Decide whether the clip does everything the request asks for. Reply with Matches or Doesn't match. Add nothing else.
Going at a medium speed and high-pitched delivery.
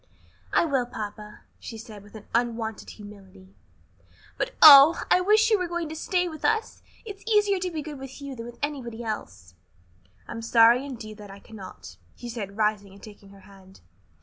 Matches